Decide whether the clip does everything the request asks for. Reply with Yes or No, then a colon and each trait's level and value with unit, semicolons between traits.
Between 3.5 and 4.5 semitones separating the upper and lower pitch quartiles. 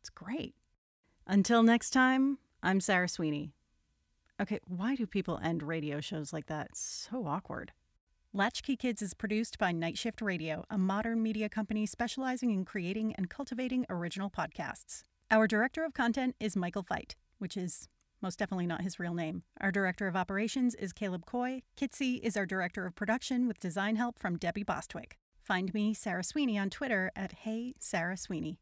Yes: average, 4.1 semitones